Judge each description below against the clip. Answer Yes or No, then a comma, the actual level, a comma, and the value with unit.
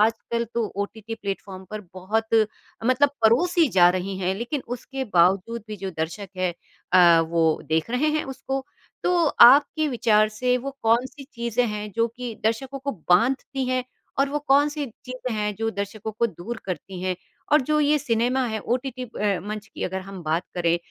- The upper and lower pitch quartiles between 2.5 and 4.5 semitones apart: No, average, 4.9 semitones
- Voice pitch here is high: Yes, high, 225 Hz